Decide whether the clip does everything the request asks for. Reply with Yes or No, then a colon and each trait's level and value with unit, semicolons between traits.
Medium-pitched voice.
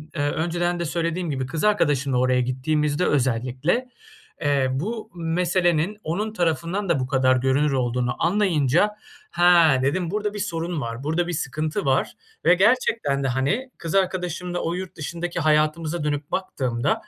Yes: medium, 160 Hz